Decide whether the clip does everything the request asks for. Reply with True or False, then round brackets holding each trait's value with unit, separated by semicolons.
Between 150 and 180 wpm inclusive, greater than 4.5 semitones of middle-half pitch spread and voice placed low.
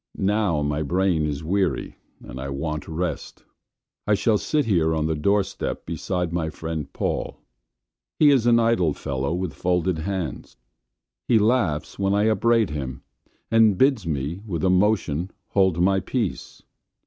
True (155 wpm; 4.9 semitones; 90 Hz)